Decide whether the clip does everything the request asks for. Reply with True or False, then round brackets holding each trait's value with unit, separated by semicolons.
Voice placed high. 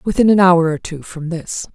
False (175 Hz)